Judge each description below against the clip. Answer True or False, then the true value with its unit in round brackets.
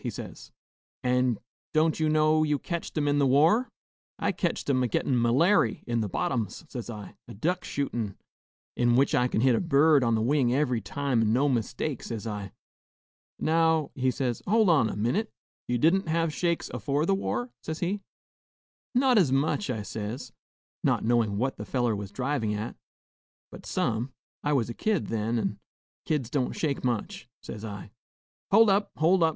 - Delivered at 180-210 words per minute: True (185 wpm)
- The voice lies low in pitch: True (130 Hz)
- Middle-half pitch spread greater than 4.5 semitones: True (5.2 semitones)